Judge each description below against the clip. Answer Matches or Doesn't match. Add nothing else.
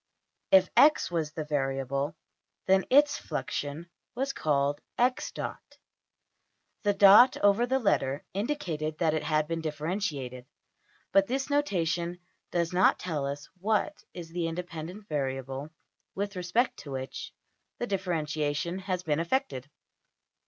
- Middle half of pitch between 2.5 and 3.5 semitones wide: Doesn't match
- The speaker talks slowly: Matches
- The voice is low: Doesn't match